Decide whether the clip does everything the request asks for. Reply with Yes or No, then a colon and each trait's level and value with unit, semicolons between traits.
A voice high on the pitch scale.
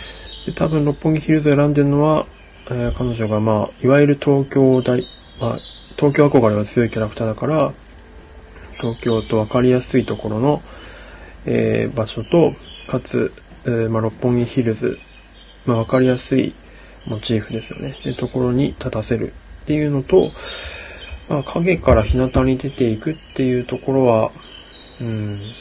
No: low, 125 Hz